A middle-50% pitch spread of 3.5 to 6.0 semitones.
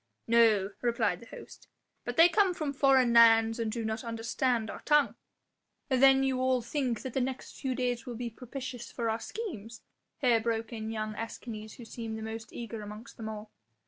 No: narrow, 2.5 semitones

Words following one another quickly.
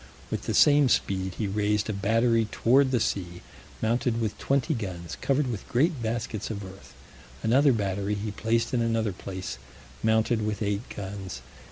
No: average, 165 wpm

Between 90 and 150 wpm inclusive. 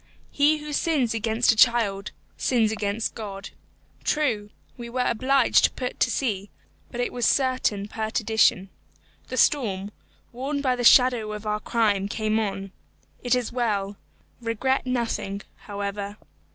Yes: average, 140 wpm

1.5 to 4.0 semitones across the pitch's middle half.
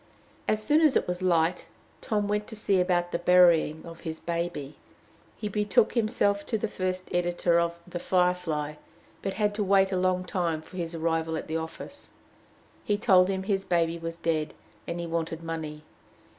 Yes: average, 2.8 semitones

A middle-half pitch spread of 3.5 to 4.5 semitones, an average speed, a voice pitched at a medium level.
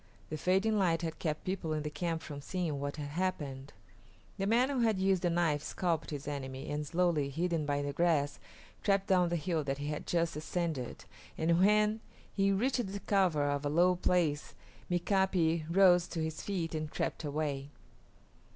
Yes: average, 3.9 semitones; average, 185 wpm; medium, 165 Hz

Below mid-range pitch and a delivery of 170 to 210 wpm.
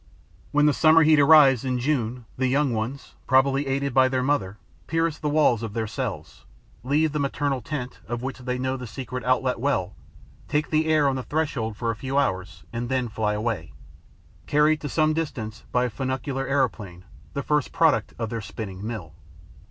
Yes: low, 130 Hz; average, 190 wpm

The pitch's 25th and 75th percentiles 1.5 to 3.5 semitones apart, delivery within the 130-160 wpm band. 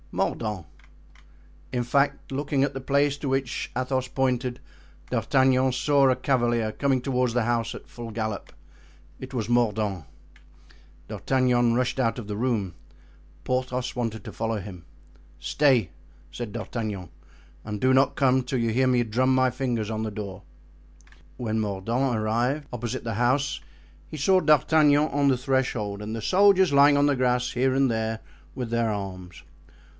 Yes: average, 3.1 semitones; average, 155 wpm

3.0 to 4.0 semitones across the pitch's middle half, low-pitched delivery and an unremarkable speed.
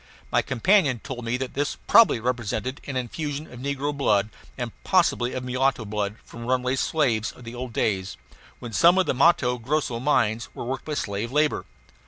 Yes: average, 3.5 semitones; low, 125 Hz; average, 185 wpm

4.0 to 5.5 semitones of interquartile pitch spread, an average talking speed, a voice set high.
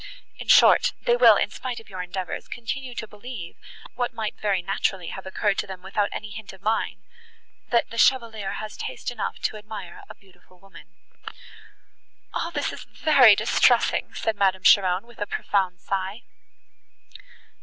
No: average, 3.5 semitones; average, 160 wpm; high, 205 Hz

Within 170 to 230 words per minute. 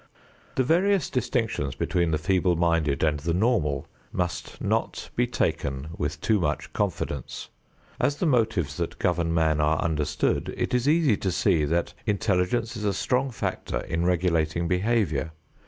No: average, 155 wpm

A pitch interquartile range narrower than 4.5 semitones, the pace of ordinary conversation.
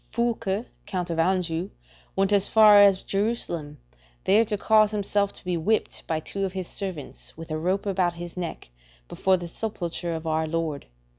Yes: average, 3.5 semitones; average, 175 wpm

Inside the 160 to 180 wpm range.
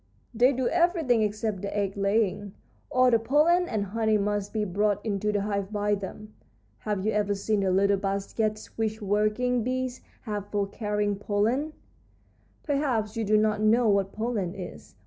Yes: average, 165 wpm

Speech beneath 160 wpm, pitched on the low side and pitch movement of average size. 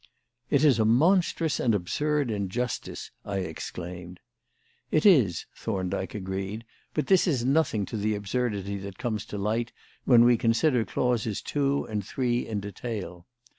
Yes: average, 145 wpm; low, 110 Hz; average, 4.4 semitones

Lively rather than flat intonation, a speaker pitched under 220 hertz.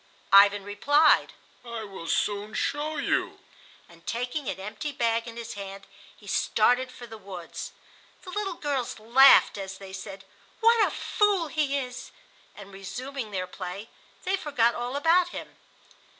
No: wide, 6.4 semitones; high, 235 Hz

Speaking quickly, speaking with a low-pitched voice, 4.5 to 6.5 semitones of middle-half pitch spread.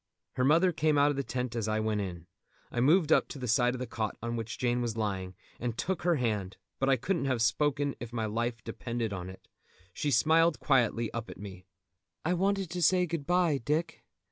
Yes: fast, 220 wpm; low, 125 Hz; wide, 5.4 semitones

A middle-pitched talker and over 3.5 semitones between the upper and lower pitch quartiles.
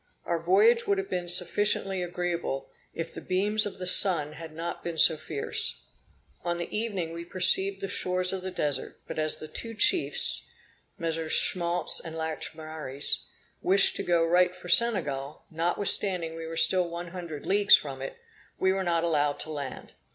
No: medium, 175 Hz; average, 2.8 semitones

